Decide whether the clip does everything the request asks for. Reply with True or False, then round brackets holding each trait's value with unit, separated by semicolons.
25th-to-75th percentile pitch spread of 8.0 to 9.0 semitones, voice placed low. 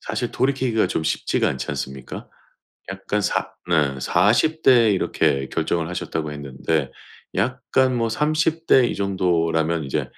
True (8.5 semitones; 90 Hz)